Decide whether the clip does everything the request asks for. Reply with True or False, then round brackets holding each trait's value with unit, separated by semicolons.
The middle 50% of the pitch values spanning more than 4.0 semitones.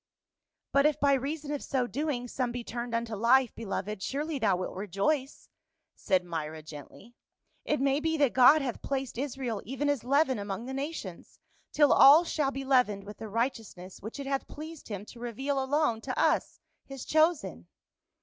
True (4.9 semitones)